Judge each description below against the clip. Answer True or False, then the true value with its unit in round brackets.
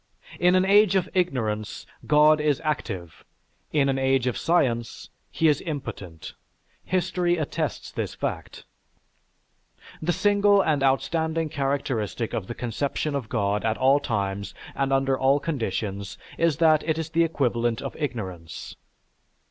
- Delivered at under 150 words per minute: True (140 wpm)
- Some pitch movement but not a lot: False (5.9 semitones)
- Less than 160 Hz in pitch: True (140 Hz)